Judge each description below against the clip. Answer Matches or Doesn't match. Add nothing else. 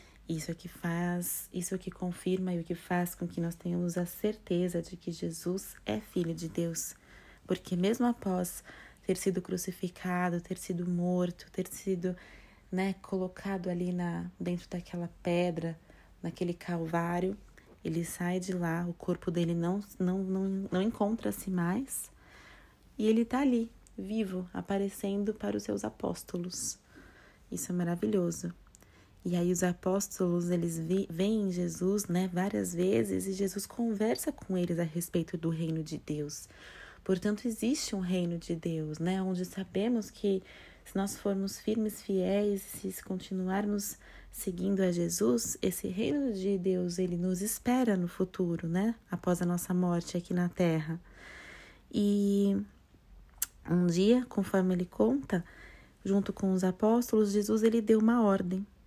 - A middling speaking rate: Matches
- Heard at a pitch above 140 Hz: Matches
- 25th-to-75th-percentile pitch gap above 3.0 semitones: Doesn't match